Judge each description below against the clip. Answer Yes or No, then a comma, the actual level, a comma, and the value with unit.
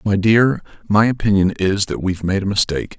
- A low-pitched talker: Yes, low, 100 Hz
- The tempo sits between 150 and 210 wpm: Yes, average, 200 wpm